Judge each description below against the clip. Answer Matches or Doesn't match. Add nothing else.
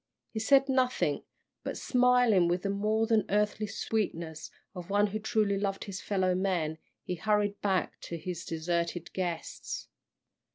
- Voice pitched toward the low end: Doesn't match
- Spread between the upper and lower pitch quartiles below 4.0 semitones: Matches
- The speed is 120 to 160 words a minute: Matches